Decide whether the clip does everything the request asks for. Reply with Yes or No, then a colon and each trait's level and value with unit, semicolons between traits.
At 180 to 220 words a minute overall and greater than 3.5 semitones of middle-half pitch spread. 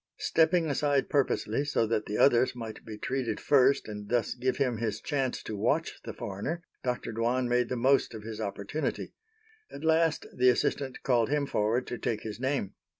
Yes: average, 185 wpm; average, 3.9 semitones